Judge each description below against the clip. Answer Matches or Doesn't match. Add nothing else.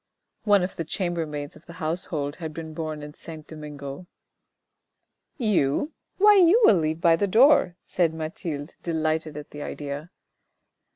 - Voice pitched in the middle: Matches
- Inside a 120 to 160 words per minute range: Matches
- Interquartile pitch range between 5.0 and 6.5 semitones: Doesn't match